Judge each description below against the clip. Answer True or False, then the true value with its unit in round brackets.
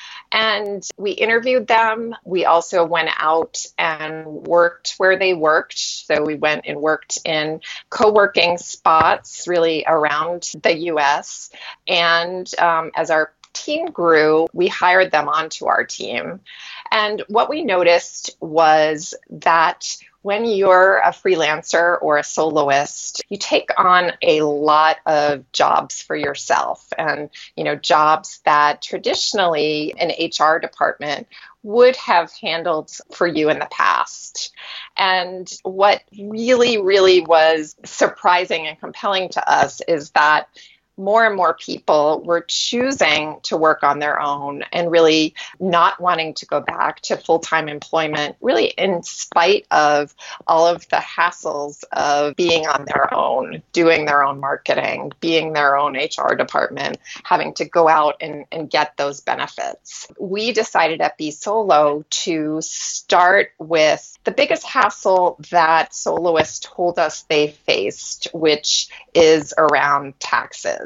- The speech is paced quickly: False (140 wpm)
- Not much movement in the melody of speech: False (3.6 semitones)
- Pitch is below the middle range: False (165 Hz)